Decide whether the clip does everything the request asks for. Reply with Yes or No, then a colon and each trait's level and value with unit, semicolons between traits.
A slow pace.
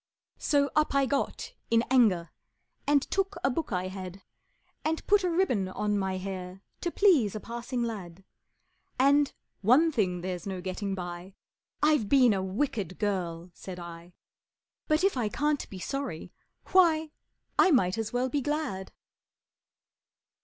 No: average, 150 wpm